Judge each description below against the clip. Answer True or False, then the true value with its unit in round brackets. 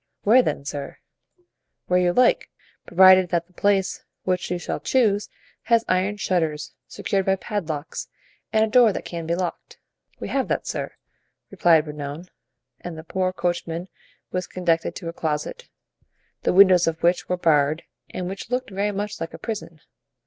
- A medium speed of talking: True (165 wpm)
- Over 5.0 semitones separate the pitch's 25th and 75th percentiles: False (3.3 semitones)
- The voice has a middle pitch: True (180 Hz)